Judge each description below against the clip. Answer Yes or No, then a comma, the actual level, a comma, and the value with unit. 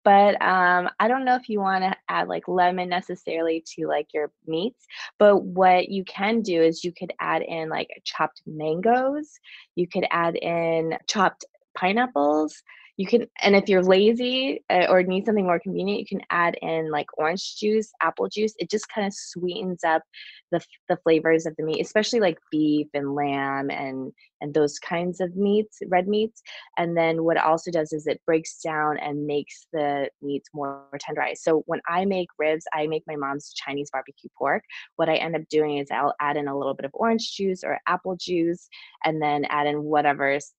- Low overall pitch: No, medium, 170 Hz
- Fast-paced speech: No, average, 195 wpm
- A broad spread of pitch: No, average, 4.3 semitones